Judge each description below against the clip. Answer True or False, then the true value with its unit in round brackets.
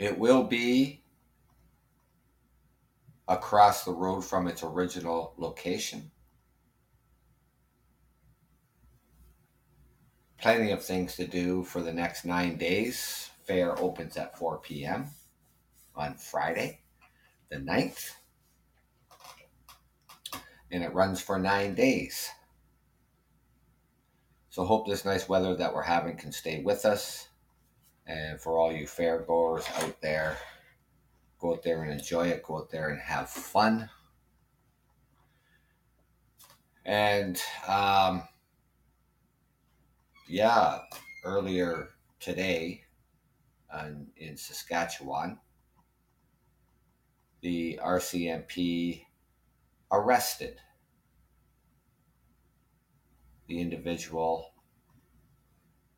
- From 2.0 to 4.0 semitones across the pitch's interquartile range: True (2.7 semitones)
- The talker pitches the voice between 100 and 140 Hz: False (90 Hz)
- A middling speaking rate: False (85 wpm)